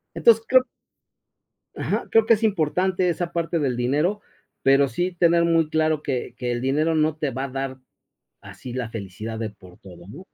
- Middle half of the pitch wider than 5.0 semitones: Yes, wide, 5.6 semitones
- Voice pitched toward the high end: No, medium, 150 Hz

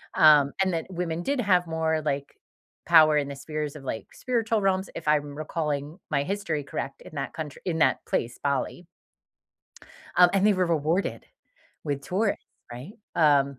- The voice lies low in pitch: No, medium, 155 Hz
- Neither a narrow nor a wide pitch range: Yes, average, 4.0 semitones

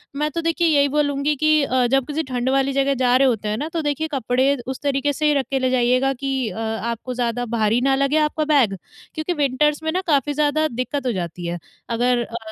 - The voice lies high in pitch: Yes, very high, 270 Hz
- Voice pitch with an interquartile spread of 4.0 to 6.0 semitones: No, average, 3.3 semitones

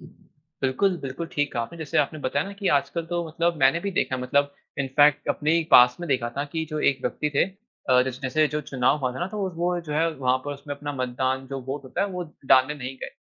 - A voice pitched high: No, medium, 145 Hz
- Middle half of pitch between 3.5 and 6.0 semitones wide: Yes, average, 3.8 semitones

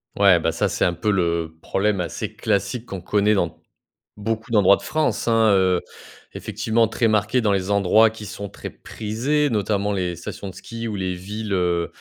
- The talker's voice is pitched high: No, low, 100 Hz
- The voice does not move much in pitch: No, average, 3.2 semitones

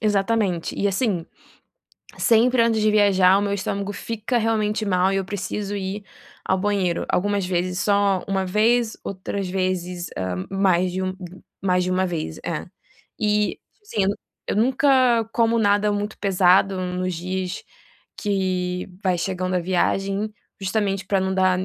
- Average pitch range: No, narrow, 2.2 semitones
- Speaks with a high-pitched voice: Yes, high, 195 Hz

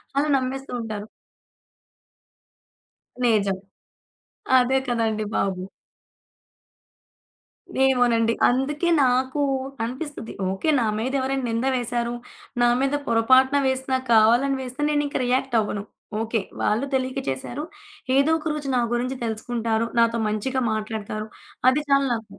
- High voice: Yes, high, 245 Hz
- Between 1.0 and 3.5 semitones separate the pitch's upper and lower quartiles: Yes, average, 2.9 semitones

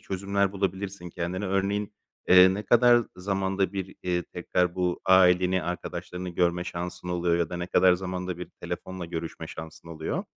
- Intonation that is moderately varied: No, narrow, 1.6 semitones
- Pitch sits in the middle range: No, very low, 90 Hz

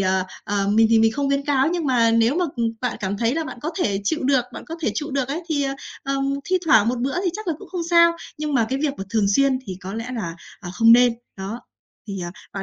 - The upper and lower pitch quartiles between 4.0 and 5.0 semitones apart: No, wide, 5.5 semitones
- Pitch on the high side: Yes, high, 245 Hz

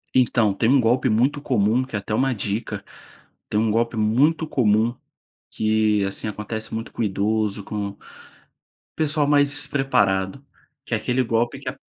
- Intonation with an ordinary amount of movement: Yes, average, 3.6 semitones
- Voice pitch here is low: Yes, low, 115 Hz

